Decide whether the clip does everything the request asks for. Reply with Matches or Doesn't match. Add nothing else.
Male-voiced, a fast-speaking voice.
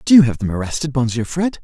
Matches